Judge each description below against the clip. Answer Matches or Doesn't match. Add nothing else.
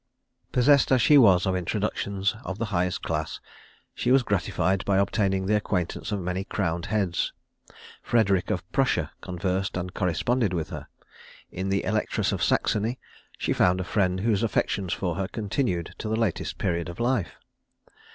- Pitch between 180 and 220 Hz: Doesn't match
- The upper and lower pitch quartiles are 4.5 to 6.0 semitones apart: Doesn't match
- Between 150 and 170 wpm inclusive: Matches